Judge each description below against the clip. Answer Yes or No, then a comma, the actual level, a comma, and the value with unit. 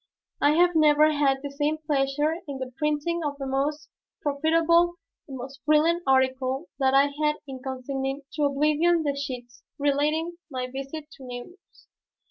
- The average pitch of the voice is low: No, very high, 290 Hz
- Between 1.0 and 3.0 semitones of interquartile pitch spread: Yes, narrow, 2.4 semitones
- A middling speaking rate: Yes, average, 155 wpm